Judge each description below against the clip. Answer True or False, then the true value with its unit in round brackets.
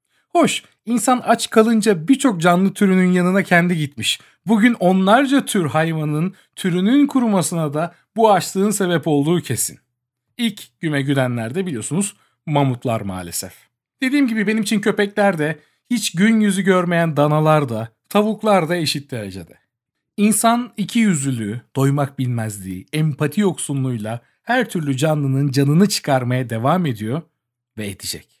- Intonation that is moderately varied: False (7.5 semitones)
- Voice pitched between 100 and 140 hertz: False (170 Hz)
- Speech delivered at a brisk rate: False (130 wpm)